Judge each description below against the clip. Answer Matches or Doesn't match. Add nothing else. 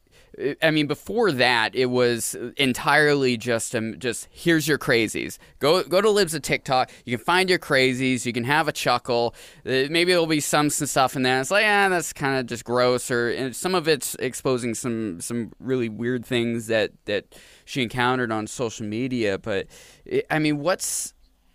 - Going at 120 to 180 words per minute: Doesn't match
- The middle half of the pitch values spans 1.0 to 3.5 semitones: Doesn't match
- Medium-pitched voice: Doesn't match